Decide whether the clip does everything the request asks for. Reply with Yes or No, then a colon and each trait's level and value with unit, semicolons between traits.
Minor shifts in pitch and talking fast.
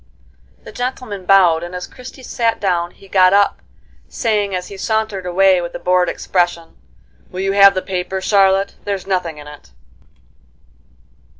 No: narrow, 2.0 semitones; average, 160 wpm